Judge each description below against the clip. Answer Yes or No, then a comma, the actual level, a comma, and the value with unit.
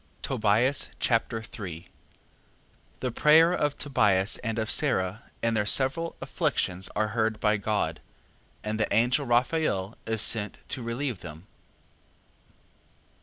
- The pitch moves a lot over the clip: No, average, 3.8 semitones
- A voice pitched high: No, low, 110 Hz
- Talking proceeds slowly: Yes, slow, 120 wpm